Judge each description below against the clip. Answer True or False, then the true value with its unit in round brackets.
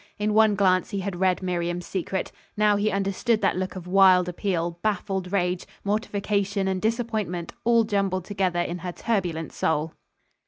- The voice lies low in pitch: False (190 Hz)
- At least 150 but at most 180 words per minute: True (160 wpm)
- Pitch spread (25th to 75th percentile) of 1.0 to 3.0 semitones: True (2.4 semitones)